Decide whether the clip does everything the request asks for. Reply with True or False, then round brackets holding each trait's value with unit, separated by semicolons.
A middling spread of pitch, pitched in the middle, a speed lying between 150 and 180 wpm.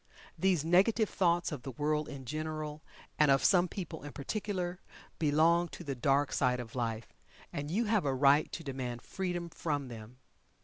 True (4.3 semitones; 150 Hz; 175 wpm)